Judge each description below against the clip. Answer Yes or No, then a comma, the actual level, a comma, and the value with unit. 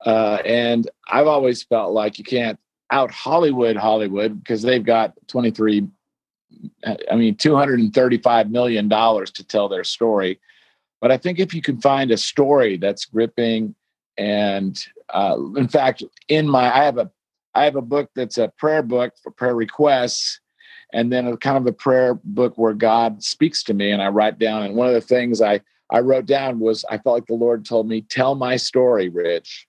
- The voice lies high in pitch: No, low, 120 Hz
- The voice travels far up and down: No, average, 3.8 semitones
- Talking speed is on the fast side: No, average, 190 wpm